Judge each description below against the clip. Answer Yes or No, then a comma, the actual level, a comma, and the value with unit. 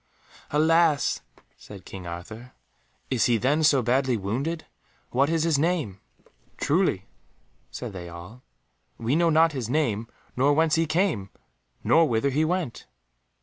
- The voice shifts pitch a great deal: Yes, wide, 6.2 semitones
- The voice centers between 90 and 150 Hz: Yes, low, 135 Hz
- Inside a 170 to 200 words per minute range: No, average, 140 wpm